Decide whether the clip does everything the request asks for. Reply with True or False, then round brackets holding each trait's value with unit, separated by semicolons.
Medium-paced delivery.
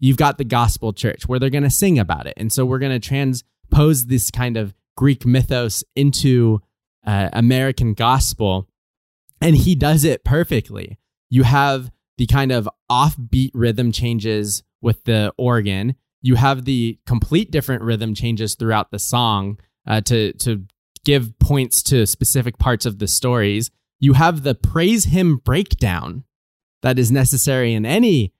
True (160 wpm)